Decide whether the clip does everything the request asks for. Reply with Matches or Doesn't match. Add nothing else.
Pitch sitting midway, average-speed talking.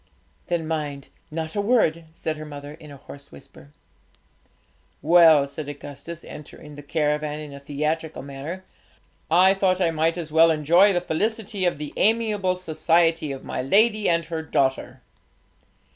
Matches